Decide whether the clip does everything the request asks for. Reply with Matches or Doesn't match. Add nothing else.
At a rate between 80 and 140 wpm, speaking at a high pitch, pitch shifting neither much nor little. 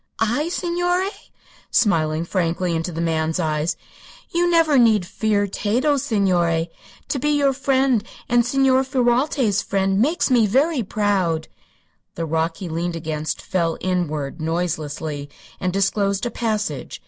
Doesn't match